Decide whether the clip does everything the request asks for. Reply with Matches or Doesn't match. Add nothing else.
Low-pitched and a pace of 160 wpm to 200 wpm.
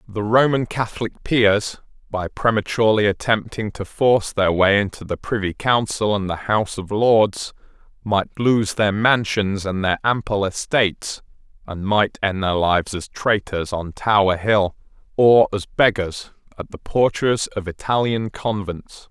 Doesn't match